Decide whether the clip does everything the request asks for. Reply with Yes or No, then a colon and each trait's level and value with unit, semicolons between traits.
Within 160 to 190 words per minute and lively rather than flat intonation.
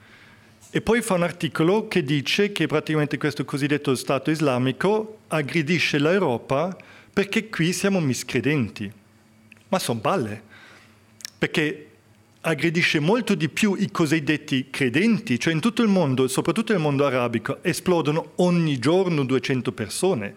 No: average, 130 wpm; wide, 6.1 semitones